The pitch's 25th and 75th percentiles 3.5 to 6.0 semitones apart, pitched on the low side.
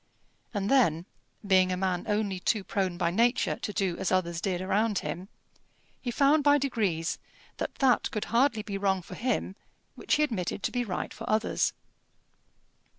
No: average, 4.2 semitones; high, 200 Hz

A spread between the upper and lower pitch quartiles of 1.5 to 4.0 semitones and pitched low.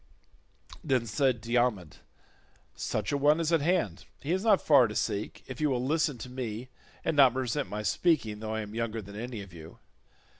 No: average, 5.1 semitones; low, 125 Hz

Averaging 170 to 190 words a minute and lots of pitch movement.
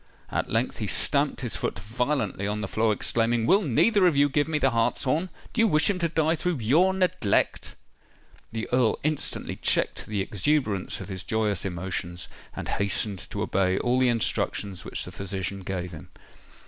Yes: average, 180 wpm; wide, 7.6 semitones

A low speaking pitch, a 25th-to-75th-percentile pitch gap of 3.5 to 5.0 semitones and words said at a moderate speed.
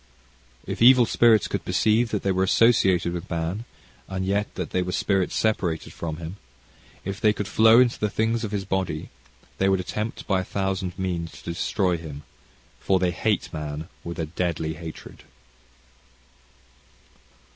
Yes: very low, 95 Hz; average, 3.8 semitones; average, 170 wpm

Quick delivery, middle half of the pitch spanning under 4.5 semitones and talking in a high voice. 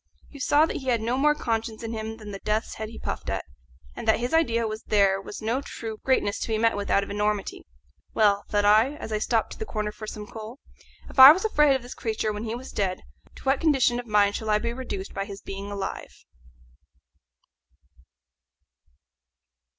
Yes: fast, 210 wpm; average, 3.0 semitones; high, 220 Hz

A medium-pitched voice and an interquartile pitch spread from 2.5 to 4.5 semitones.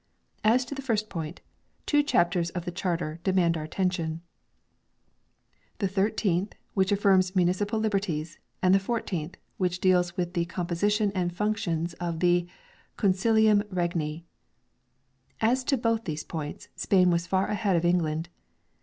Yes: medium, 180 Hz; average, 3.3 semitones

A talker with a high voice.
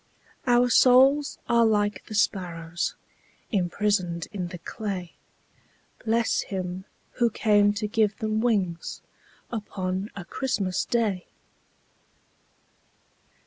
Yes: high, 205 Hz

